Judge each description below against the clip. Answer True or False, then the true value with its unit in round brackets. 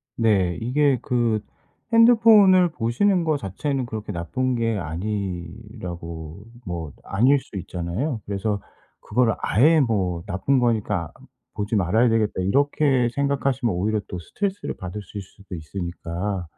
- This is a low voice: True (110 Hz)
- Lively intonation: True (6.4 semitones)